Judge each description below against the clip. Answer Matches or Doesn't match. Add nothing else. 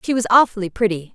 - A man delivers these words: Doesn't match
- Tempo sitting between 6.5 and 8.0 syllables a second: Matches